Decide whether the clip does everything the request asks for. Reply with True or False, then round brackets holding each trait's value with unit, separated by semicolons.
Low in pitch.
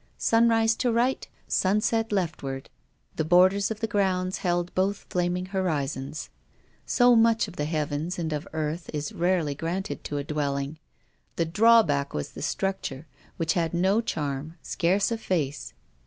False (175 Hz)